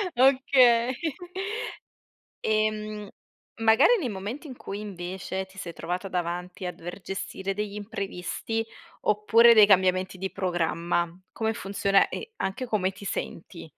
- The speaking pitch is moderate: No, high, 200 Hz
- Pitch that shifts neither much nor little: Yes, average, 3.2 semitones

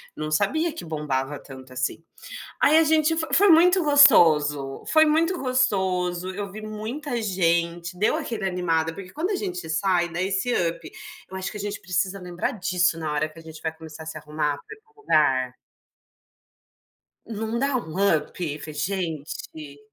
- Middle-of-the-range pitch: Yes, medium, 180 Hz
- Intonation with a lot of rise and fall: Yes, wide, 7.7 semitones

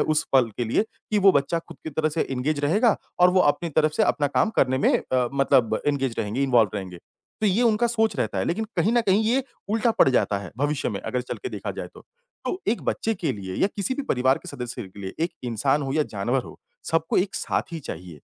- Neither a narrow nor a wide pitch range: No, wide, 7.6 semitones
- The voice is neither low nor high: Yes, medium, 145 Hz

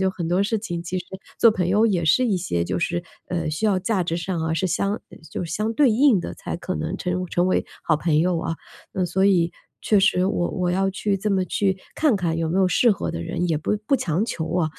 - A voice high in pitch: No, medium, 180 Hz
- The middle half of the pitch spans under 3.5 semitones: Yes, average, 2.9 semitones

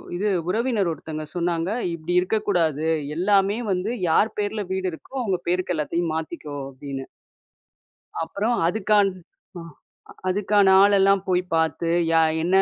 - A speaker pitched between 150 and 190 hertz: Yes, medium, 185 Hz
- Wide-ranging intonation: No, average, 3.9 semitones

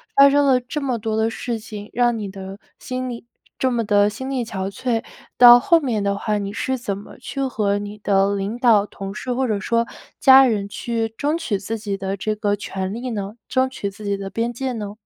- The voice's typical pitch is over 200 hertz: Yes, high, 220 Hz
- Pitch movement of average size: Yes, average, 3.6 semitones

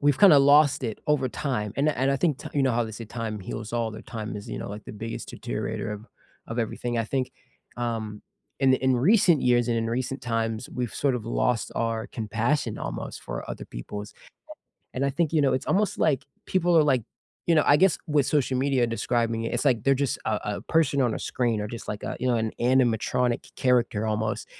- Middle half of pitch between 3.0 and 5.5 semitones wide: Yes, average, 3.5 semitones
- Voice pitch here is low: Yes, low, 120 Hz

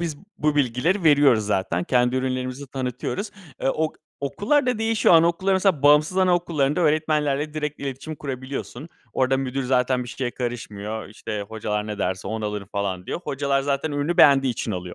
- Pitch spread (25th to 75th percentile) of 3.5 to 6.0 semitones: Yes, average, 4.2 semitones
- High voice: No, low, 135 Hz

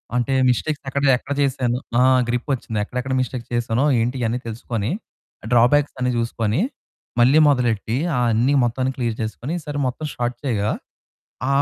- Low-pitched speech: Yes, low, 125 Hz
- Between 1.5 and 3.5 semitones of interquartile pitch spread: Yes, narrow, 2.4 semitones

